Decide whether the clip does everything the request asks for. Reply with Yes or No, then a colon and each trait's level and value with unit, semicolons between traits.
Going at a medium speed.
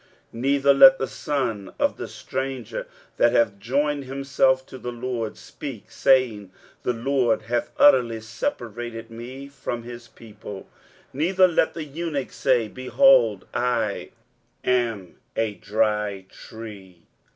No: slow, 130 wpm